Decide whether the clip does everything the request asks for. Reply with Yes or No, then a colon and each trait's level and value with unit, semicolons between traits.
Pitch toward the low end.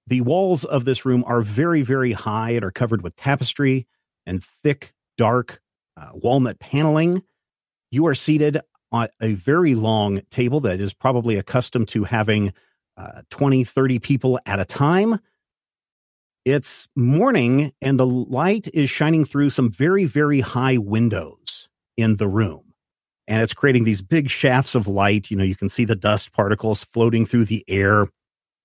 Yes: low, 125 Hz